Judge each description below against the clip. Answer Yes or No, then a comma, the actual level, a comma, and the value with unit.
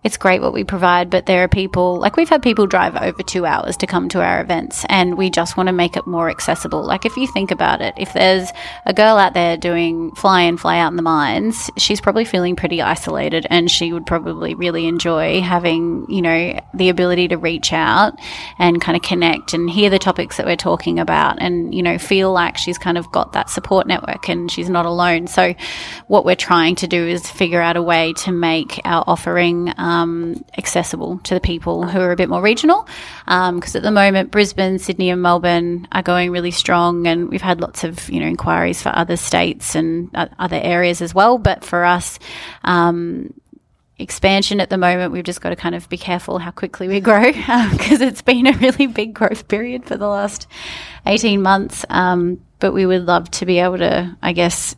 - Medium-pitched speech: Yes, medium, 180 Hz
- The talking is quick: Yes, fast, 220 wpm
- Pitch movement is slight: Yes, narrow, 2.3 semitones